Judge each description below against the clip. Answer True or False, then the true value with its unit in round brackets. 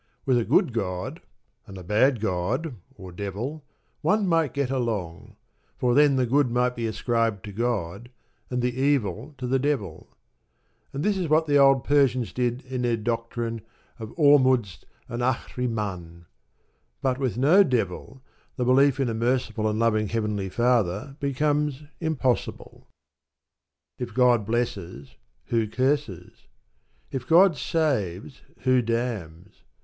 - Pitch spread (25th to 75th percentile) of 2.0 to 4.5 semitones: True (4.2 semitones)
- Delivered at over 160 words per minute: False (140 wpm)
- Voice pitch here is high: False (120 Hz)